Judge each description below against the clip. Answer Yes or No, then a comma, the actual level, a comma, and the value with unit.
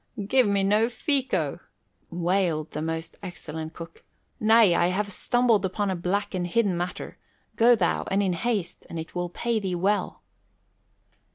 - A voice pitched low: No, high, 190 Hz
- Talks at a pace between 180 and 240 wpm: No, average, 160 wpm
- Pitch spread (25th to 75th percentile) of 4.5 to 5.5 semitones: No, average, 3.8 semitones